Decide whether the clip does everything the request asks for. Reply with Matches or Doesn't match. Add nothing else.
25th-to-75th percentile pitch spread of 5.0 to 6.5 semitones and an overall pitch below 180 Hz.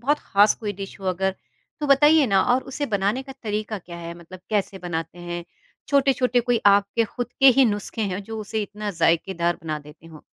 Doesn't match